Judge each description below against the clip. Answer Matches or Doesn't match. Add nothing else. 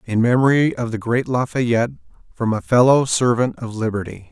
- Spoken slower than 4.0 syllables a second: Doesn't match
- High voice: Doesn't match